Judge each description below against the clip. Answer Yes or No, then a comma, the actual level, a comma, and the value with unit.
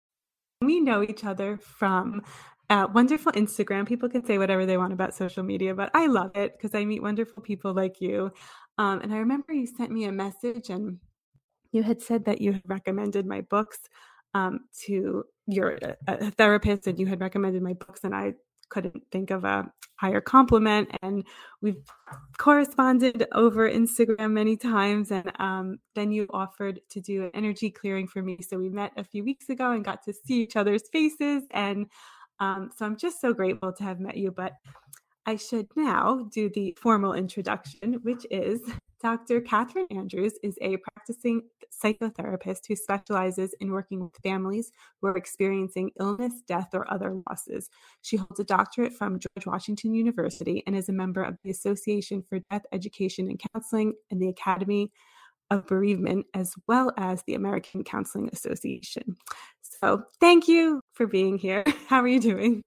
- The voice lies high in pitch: Yes, high, 205 Hz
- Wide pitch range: No, average, 3.3 semitones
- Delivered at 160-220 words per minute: Yes, average, 175 wpm